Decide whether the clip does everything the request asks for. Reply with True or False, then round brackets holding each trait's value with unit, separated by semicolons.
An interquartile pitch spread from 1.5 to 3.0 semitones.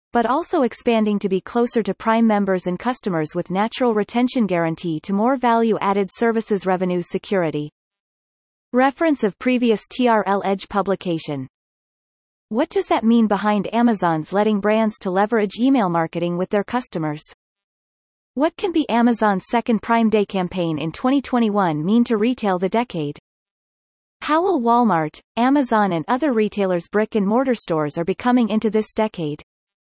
False (4.3 semitones)